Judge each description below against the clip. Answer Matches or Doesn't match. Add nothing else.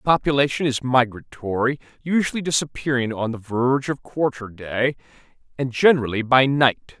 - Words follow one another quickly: Doesn't match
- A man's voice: Matches